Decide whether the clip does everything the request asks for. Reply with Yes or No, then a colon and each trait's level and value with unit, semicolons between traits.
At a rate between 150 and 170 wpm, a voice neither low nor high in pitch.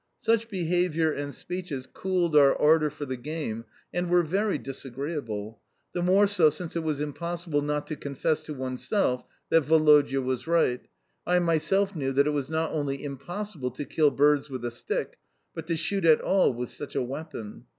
No: average, 180 wpm; medium, 150 Hz